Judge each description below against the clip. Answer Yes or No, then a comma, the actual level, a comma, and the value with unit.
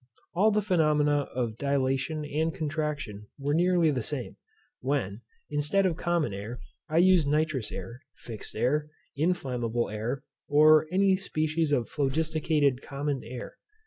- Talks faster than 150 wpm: No, slow, 135 wpm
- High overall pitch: No, medium, 145 Hz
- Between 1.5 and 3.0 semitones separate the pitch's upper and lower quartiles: No, average, 3.9 semitones